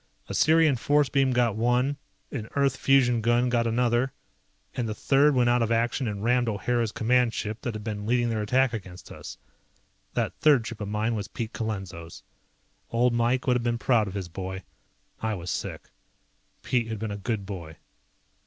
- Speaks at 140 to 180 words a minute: No, average, 190 wpm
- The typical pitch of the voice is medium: No, low, 115 Hz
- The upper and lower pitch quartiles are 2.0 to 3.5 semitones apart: Yes, average, 2.8 semitones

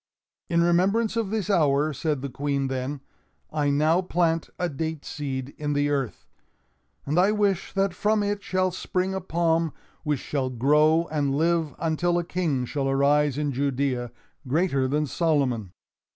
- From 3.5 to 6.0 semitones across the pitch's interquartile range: Yes, average, 3.9 semitones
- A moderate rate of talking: Yes, average, 160 wpm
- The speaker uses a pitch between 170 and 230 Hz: No, medium, 155 Hz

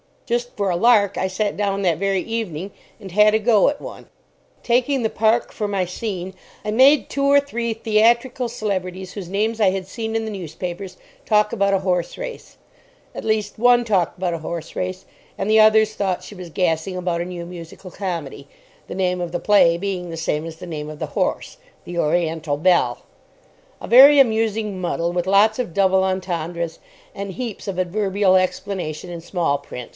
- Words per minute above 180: Yes, average, 190 wpm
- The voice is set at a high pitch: Yes, high, 195 Hz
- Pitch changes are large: No, average, 3.7 semitones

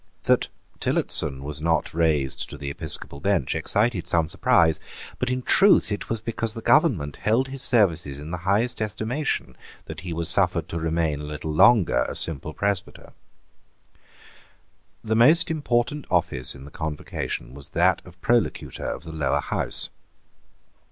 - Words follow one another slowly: No, average, 155 wpm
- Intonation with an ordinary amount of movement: No, wide, 7.0 semitones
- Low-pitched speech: Yes, very low, 85 Hz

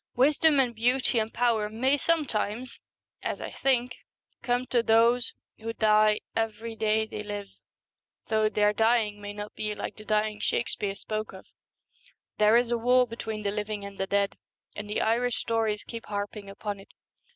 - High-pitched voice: Yes, high, 220 Hz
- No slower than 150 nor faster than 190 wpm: Yes, average, 170 wpm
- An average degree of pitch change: No, narrow, 2.3 semitones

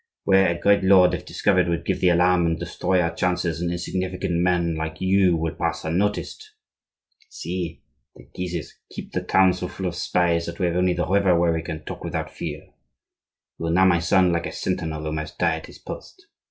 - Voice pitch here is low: Yes, very low, 90 Hz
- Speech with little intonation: Yes, narrow, 1.8 semitones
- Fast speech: Yes, fast, 210 wpm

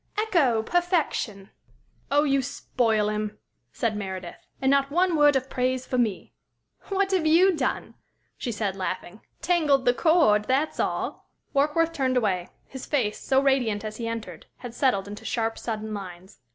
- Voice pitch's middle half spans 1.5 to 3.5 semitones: No, wide, 5.6 semitones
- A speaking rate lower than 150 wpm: No, average, 160 wpm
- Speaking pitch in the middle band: No, very high, 250 Hz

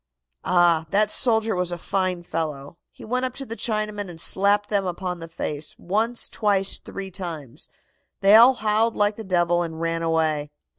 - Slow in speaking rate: No, average, 180 wpm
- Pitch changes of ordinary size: Yes, average, 4.2 semitones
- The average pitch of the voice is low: No, high, 190 Hz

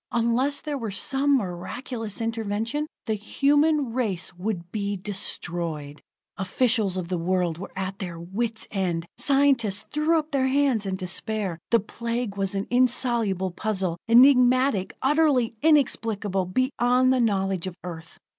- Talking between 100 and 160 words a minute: Yes, slow, 135 wpm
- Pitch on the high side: Yes, high, 220 Hz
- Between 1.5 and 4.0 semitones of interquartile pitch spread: No, average, 5.3 semitones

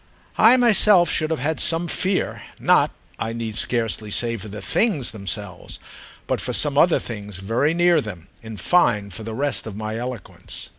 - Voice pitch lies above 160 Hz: No, low, 115 Hz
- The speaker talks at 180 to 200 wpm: No, average, 170 wpm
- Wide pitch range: Yes, wide, 7.7 semitones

